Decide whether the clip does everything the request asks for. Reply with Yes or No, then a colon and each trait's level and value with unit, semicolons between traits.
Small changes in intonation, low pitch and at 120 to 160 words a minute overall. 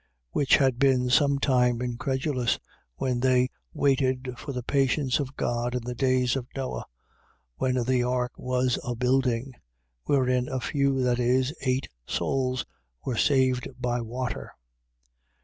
Yes: narrow, 1.3 semitones; low, 130 Hz; average, 140 wpm